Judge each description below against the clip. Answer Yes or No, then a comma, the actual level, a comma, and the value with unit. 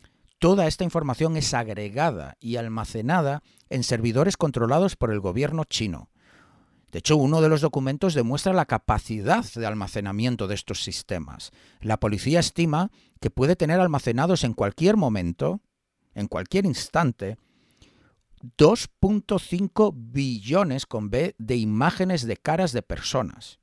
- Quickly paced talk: No, average, 130 wpm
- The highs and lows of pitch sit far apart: Yes, wide, 7.5 semitones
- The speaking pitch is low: Yes, low, 125 Hz